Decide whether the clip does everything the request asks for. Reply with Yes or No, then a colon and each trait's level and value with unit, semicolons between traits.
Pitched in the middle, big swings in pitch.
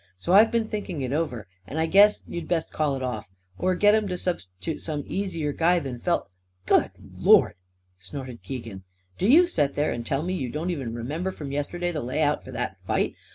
Yes: medium, 155 Hz; wide, 5.9 semitones